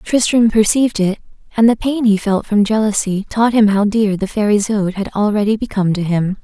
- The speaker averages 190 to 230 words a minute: Yes, fast, 205 wpm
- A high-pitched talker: Yes, high, 210 Hz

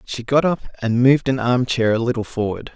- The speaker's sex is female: No, male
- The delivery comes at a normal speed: No, fast, 240 wpm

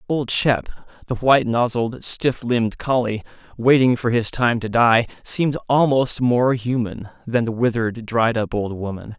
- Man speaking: Yes, male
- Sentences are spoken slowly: No, average, 165 wpm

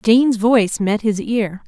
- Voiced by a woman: Yes, female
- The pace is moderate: Yes, average, 180 wpm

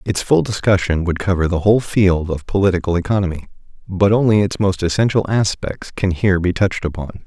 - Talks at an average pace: Yes, average, 180 wpm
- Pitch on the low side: Yes, very low, 95 Hz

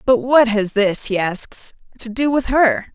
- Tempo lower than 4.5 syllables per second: Yes, 3.9 syllables/s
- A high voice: Yes, high, 240 Hz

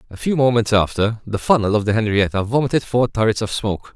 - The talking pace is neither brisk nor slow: No, fast, 210 wpm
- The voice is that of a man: Yes, male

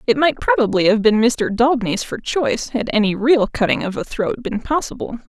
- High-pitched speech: Yes, high, 235 Hz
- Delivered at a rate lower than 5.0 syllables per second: No, 5.4 syllables/s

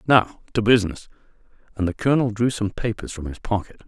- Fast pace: No, average, 185 wpm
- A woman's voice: No, male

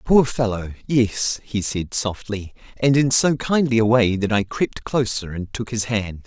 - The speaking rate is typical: Yes, average, 190 wpm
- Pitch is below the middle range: Yes, low, 115 Hz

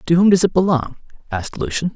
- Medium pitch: Yes, medium, 165 Hz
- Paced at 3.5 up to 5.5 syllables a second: No, 6.8 syllables/s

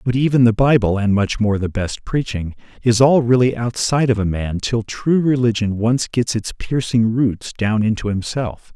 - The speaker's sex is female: No, male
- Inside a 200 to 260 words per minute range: No, average, 190 wpm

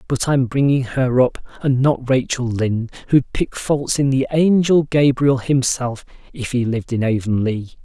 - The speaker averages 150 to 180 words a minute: Yes, average, 170 wpm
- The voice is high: No, low, 130 Hz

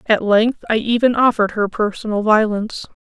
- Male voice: No, female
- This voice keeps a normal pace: Yes, average, 160 wpm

